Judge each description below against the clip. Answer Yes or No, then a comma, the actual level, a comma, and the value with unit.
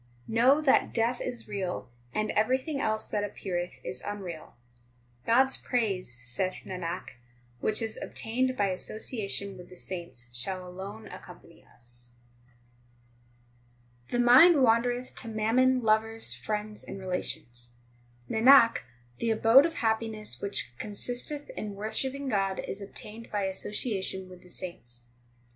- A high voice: Yes, high, 215 Hz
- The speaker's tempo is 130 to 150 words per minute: Yes, average, 140 wpm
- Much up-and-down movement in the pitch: No, average, 4.4 semitones